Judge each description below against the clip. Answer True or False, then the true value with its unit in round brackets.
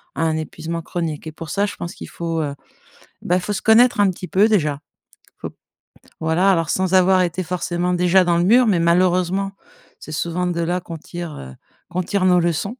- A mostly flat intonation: True (2.1 semitones)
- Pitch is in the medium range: True (175 Hz)